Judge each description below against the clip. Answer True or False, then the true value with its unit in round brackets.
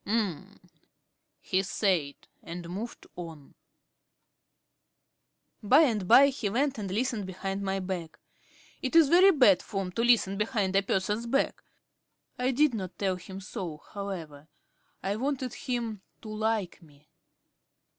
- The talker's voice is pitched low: False (200 Hz)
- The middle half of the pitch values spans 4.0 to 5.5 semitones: True (4.5 semitones)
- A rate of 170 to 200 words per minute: False (135 wpm)